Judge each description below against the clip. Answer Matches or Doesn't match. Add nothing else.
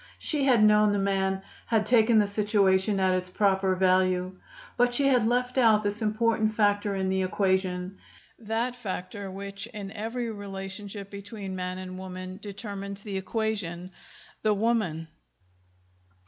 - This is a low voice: Doesn't match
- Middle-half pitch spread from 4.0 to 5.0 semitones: Doesn't match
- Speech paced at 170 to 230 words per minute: Doesn't match